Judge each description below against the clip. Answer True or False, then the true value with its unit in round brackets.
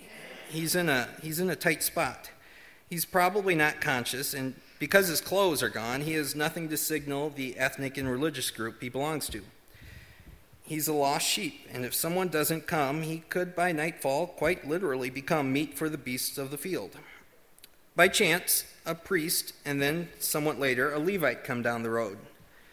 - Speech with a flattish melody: False (3.5 semitones)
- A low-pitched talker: False (150 Hz)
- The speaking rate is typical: True (180 wpm)